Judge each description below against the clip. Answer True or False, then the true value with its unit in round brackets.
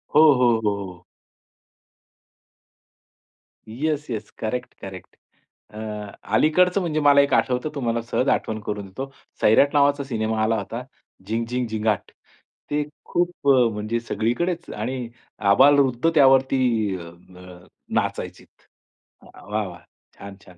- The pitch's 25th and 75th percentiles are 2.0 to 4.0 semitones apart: False (4.8 semitones)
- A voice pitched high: False (120 Hz)